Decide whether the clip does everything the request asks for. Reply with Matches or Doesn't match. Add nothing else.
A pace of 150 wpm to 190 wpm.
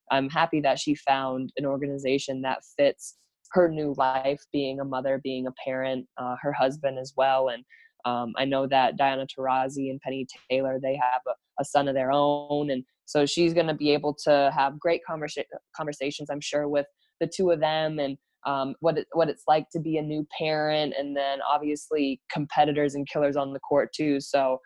Doesn't match